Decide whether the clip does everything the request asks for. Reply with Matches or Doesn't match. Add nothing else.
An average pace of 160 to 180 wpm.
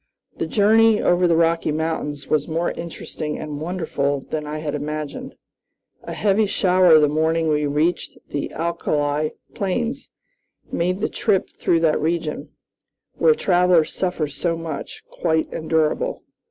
Doesn't match